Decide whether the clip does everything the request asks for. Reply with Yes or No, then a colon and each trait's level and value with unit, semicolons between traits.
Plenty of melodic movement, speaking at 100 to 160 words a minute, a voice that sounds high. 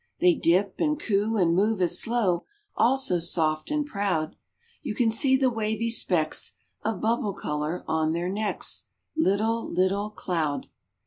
No: average, 4.6 semitones; average, 150 wpm; high, 200 Hz